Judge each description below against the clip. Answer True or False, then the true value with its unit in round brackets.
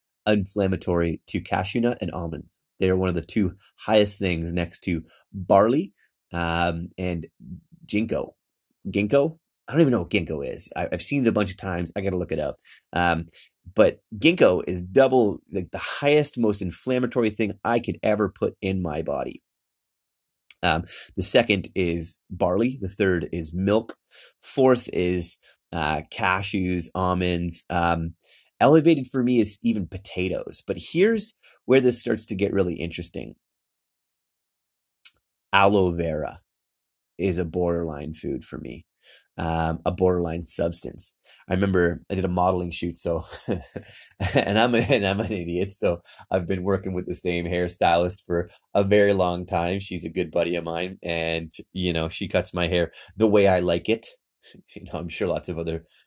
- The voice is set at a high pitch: False (90 Hz)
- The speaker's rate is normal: True (165 wpm)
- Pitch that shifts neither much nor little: True (3.2 semitones)